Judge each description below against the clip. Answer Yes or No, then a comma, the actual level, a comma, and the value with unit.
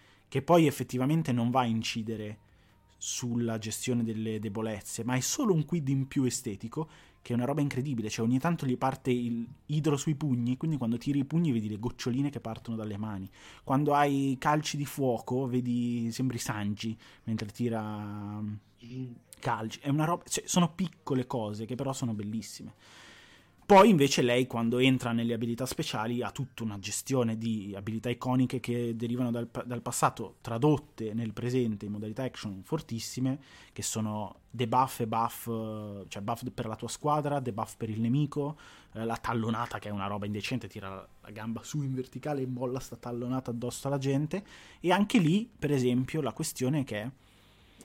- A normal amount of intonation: Yes, average, 3.5 semitones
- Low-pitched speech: Yes, low, 120 Hz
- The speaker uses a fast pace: Yes, fast, 175 wpm